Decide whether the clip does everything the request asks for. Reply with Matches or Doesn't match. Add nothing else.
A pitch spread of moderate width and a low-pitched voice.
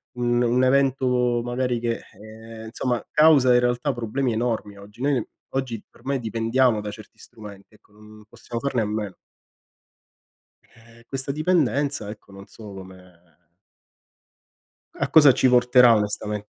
Matches